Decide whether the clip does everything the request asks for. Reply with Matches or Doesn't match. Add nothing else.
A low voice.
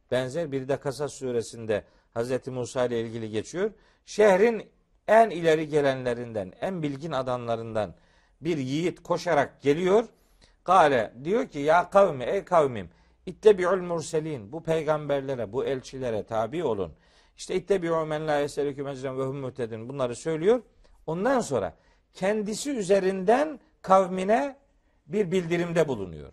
Doesn't match